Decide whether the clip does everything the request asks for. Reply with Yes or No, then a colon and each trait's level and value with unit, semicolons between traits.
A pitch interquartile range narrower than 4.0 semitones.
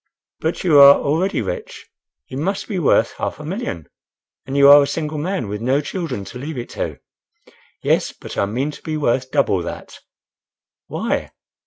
No: average, 4.3 semitones